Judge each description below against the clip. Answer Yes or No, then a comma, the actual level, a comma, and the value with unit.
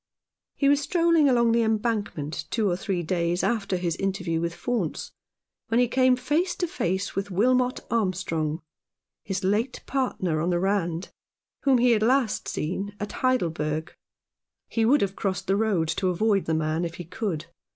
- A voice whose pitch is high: Yes, high, 200 Hz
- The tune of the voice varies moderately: No, wide, 5.7 semitones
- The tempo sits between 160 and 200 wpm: Yes, average, 170 wpm